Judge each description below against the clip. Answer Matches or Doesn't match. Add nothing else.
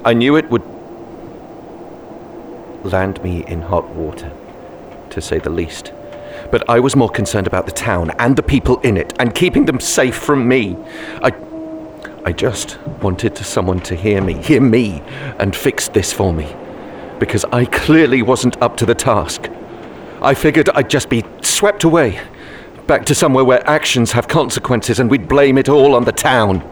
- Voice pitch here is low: Matches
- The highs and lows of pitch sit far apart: Matches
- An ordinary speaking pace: Matches